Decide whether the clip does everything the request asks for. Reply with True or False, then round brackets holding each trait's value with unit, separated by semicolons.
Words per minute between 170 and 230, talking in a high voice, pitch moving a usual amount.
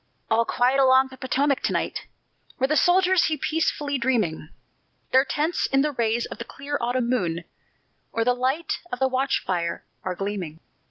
True (175 wpm; 260 Hz; 3.8 semitones)